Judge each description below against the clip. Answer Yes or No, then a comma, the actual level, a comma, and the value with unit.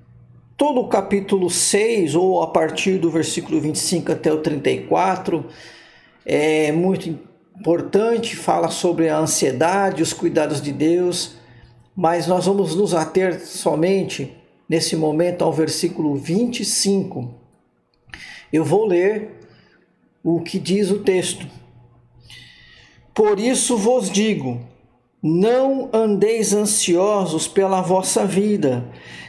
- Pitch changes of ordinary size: Yes, average, 4.1 semitones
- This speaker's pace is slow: Yes, slow, 110 wpm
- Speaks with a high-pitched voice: No, medium, 175 Hz